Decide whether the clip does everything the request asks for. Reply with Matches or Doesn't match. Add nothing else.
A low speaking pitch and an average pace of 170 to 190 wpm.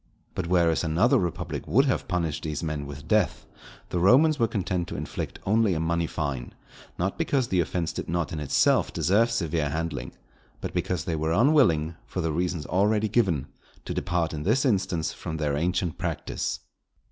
Matches